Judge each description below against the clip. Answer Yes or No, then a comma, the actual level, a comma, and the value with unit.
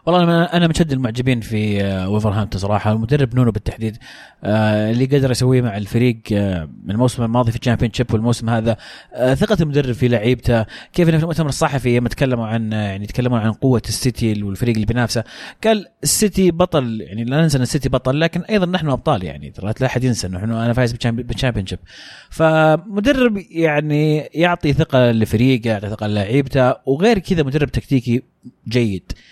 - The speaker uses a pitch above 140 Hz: No, low, 125 Hz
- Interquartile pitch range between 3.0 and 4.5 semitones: No, average, 5.1 semitones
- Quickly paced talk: Yes, fast, 160 wpm